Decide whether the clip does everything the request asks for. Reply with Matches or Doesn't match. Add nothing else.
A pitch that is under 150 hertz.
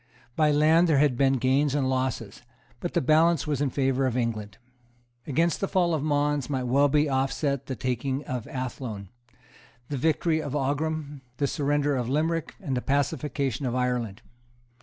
Matches